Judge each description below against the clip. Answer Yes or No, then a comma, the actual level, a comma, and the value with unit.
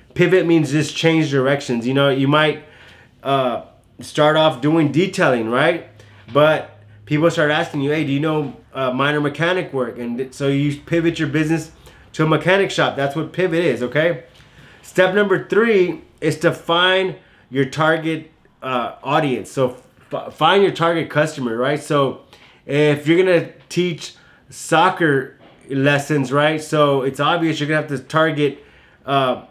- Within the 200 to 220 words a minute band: No, average, 155 wpm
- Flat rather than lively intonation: No, average, 3.2 semitones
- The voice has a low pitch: No, medium, 150 Hz